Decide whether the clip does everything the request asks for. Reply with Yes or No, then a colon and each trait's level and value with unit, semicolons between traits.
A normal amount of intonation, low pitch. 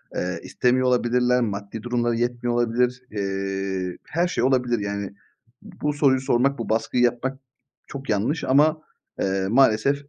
Yes: average, 3.7 semitones; low, 120 Hz